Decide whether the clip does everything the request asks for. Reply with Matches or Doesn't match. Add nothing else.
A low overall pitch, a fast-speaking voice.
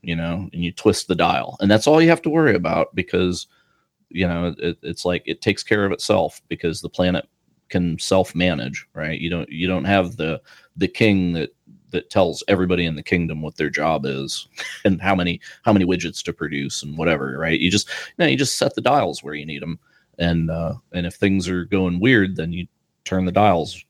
Matches